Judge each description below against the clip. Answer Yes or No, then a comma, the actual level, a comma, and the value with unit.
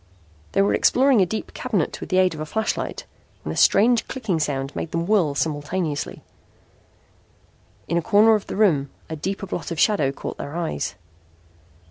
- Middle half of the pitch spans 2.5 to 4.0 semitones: No, wide, 5.4 semitones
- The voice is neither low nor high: Yes, medium, 180 Hz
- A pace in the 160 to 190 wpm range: Yes, average, 175 wpm